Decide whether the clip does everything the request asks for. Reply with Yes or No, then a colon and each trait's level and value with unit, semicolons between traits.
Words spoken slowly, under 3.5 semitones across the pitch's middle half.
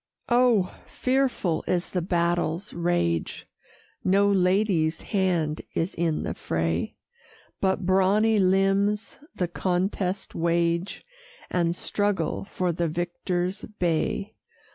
Yes: slow, 100 wpm; average, 2.7 semitones